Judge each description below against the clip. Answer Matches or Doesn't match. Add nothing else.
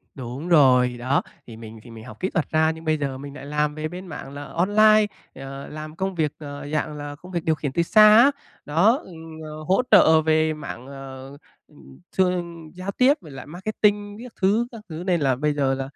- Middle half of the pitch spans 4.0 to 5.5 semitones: Matches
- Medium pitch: Matches